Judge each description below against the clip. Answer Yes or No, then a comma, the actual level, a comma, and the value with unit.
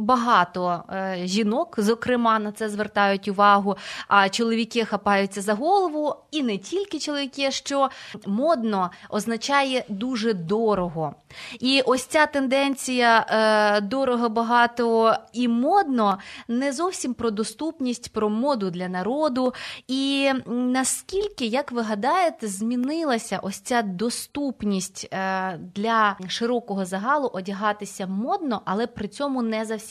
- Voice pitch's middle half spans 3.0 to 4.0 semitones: No, average, 4.5 semitones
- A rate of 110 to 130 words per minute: Yes, average, 120 wpm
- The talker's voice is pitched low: No, high, 230 Hz